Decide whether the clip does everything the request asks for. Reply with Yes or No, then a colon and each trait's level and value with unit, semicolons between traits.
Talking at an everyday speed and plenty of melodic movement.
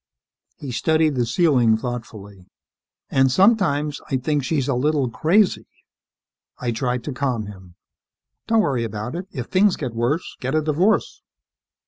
No: average, 145 wpm; average, 4.8 semitones